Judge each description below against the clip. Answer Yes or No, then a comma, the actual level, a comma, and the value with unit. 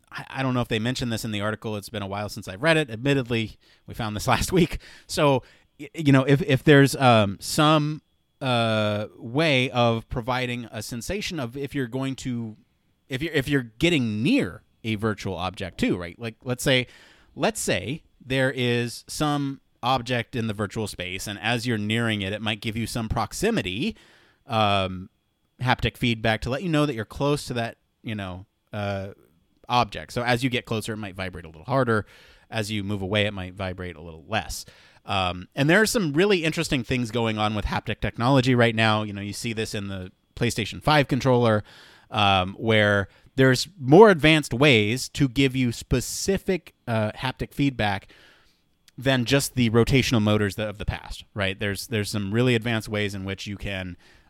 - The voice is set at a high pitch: No, low, 115 Hz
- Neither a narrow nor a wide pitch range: Yes, average, 4.1 semitones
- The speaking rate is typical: Yes, average, 190 wpm